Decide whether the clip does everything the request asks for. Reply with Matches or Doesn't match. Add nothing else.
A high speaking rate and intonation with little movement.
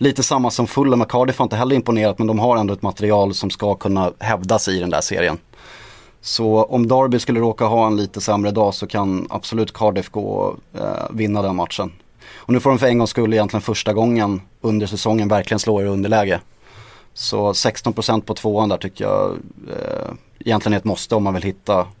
Matches